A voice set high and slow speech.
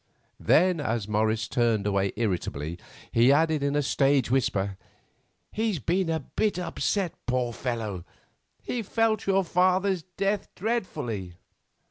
No: medium, 140 Hz; slow, 125 wpm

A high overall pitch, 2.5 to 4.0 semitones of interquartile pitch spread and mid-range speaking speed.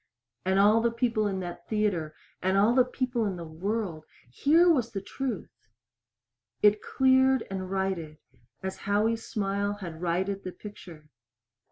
Yes: high, 200 Hz; average, 3.6 semitones; average, 150 wpm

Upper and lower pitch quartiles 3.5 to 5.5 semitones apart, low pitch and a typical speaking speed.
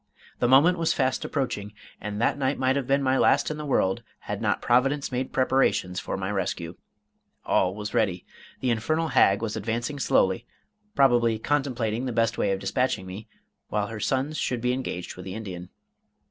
Yes: average, 4.7 semitones; low, 120 Hz; average, 185 wpm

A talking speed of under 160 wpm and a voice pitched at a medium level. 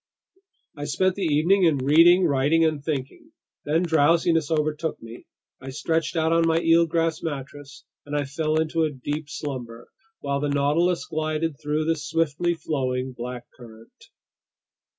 Yes: average, 150 wpm; medium, 155 Hz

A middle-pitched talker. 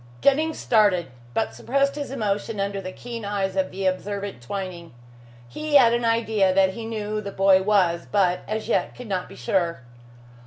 No: high, 200 Hz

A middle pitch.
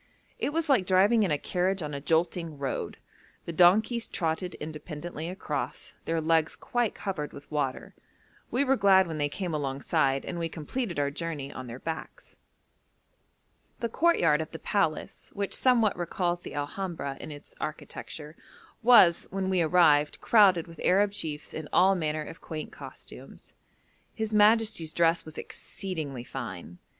Yes: medium, 165 Hz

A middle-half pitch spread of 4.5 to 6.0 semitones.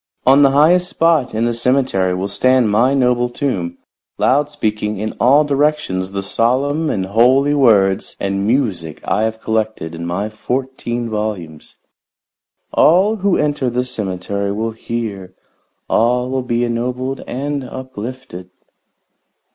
Yes: average, 4.9 semitones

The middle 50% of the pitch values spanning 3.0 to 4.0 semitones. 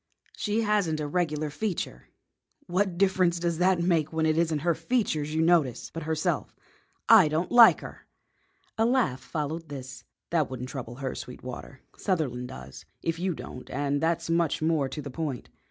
Yes: average, 3.6 semitones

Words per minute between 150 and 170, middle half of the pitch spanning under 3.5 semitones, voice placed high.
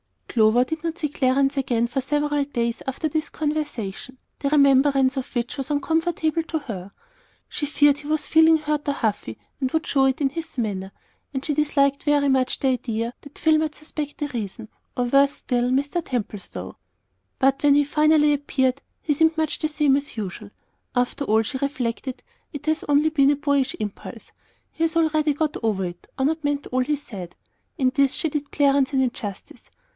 No: average, 190 wpm; average, 3.0 semitones; very high, 280 Hz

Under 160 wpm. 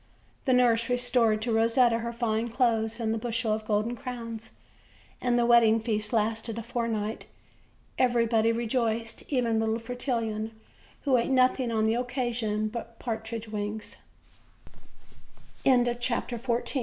Yes: average, 145 wpm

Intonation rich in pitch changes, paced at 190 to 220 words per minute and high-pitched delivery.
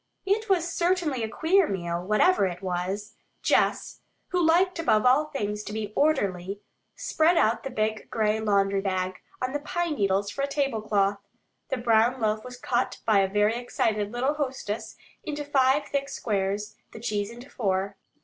No: wide, 6.0 semitones; average, 170 wpm; high, 225 Hz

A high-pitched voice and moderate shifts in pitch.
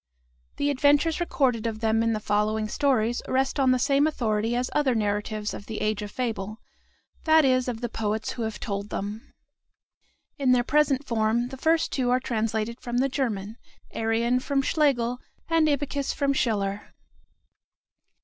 Yes: high, 240 Hz; average, 4.0 semitones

